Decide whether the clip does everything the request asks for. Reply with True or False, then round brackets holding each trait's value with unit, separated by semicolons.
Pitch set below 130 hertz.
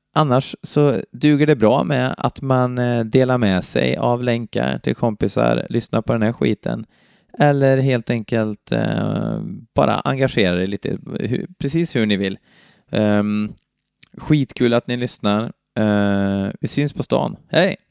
True (120 Hz)